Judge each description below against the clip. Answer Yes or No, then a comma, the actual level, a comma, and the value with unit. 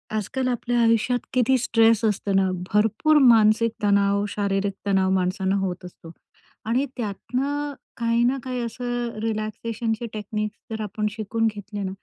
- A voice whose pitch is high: Yes, high, 220 Hz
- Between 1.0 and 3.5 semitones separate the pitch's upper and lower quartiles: Yes, average, 2.9 semitones